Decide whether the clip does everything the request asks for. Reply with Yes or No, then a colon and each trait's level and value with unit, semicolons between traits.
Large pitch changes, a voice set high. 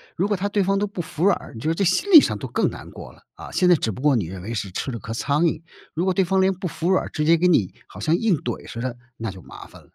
No: wide, 7.9 semitones; medium, 165 Hz